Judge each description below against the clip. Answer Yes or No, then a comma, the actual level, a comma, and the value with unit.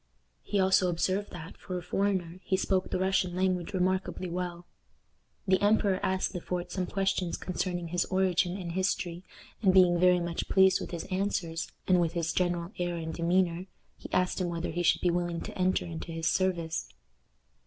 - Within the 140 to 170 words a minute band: No, average, 185 wpm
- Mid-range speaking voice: Yes, medium, 180 Hz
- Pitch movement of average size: No, narrow, 1.6 semitones